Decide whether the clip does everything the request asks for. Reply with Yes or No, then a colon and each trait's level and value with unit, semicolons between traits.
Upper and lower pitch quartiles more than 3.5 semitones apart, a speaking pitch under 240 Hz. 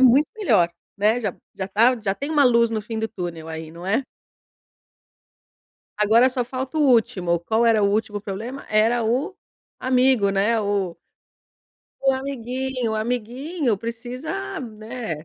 Yes: average, 4.0 semitones; high, 230 Hz